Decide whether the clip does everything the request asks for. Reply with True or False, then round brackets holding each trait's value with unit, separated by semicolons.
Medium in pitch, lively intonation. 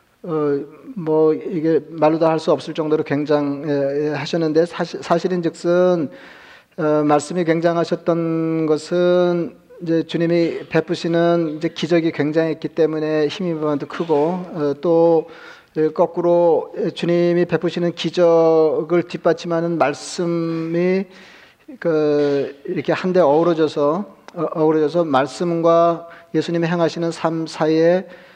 False (165 Hz; 1.8 semitones)